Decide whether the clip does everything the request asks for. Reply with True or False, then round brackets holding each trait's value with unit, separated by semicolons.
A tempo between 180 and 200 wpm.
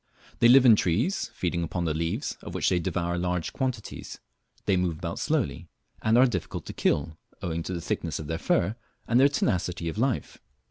True (195 wpm)